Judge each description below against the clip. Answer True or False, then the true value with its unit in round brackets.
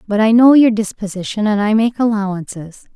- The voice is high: True (210 Hz)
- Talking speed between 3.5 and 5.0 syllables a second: False (5.5 syllables/s)